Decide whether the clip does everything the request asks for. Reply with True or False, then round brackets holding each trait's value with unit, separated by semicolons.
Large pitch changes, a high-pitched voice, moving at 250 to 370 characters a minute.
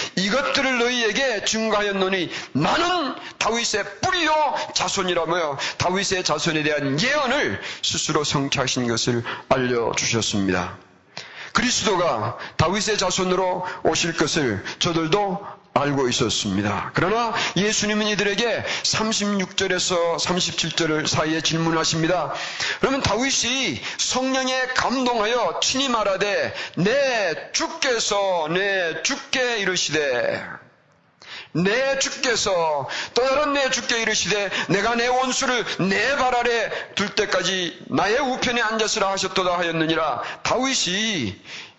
True (6.9 semitones; 200 Hz; 265 characters per minute)